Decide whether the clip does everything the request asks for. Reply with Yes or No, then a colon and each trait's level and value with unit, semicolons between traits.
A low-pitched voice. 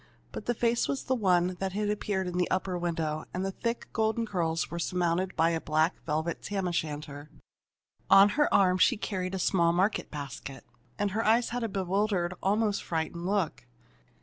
No: medium, 185 Hz